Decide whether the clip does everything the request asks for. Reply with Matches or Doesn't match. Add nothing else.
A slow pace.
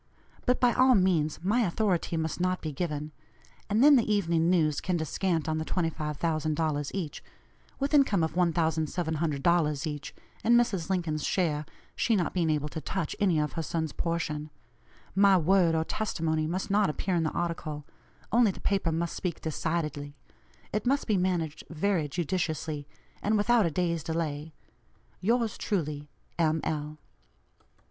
Doesn't match